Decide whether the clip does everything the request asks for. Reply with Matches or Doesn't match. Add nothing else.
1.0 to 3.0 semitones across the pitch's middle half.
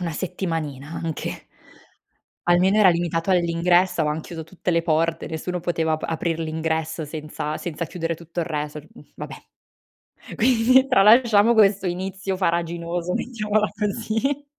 Doesn't match